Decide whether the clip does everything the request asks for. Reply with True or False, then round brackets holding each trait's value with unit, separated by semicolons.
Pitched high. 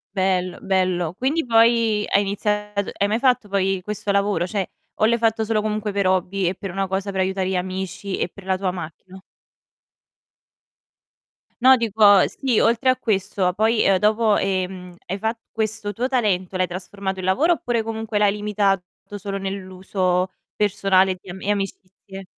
True (200 Hz)